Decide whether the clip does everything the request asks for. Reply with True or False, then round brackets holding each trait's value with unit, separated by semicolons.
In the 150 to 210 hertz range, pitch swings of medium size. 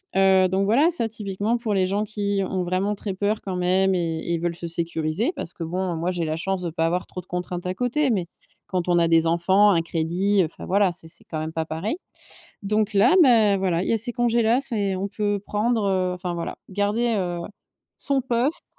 True (190 Hz; 3.4 semitones)